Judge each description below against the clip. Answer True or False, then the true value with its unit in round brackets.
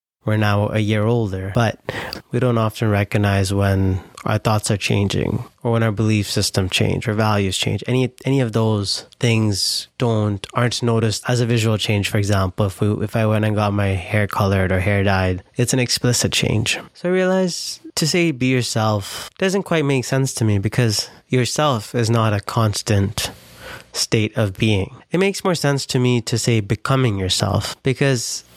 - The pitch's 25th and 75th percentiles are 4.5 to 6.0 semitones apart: False (3.3 semitones)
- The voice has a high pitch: False (110 Hz)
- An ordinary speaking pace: True (185 wpm)